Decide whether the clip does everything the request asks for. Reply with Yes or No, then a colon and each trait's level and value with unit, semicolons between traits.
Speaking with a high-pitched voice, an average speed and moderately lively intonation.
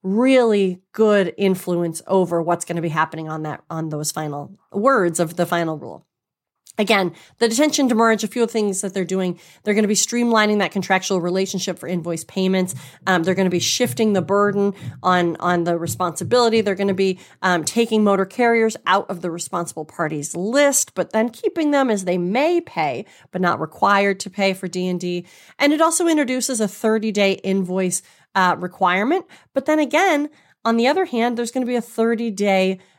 Yes: high, 195 Hz; average, 190 wpm; average, 4.3 semitones